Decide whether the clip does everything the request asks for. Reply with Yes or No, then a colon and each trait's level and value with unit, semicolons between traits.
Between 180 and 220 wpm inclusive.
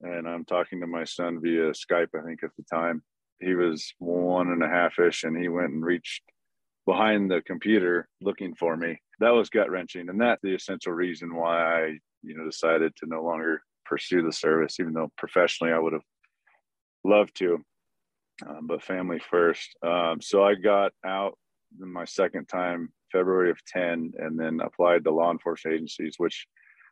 Yes: average, 185 wpm